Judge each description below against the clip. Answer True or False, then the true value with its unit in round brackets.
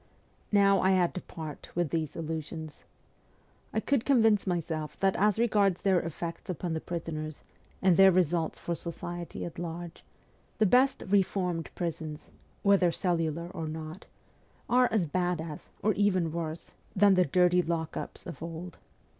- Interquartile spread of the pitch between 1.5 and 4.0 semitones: True (2.9 semitones)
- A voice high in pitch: False (175 Hz)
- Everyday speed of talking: True (155 wpm)